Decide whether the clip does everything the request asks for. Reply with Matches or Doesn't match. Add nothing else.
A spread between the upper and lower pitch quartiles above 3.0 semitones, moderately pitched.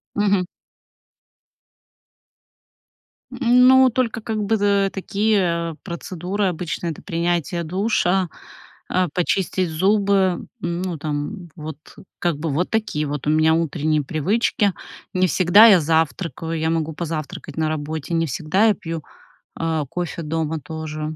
Matches